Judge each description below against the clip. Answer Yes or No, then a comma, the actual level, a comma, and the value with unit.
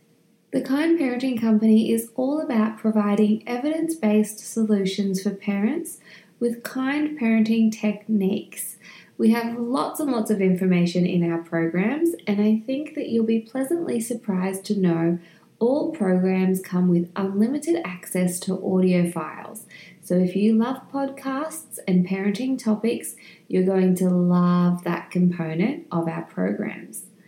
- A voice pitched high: Yes, high, 210 Hz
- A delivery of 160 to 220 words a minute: No, average, 140 wpm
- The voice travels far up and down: No, average, 4.5 semitones